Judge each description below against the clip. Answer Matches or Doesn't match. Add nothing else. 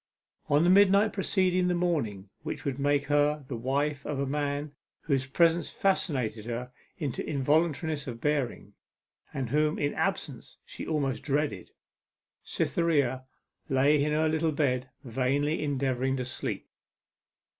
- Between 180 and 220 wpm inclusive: Doesn't match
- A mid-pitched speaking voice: Matches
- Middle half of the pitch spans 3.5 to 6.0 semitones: Doesn't match